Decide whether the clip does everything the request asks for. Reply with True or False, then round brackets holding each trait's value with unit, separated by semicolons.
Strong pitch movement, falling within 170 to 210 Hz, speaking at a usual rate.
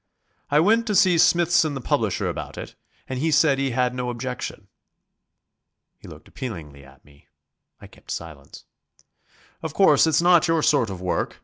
False (7.6 semitones; 135 Hz; 170 wpm)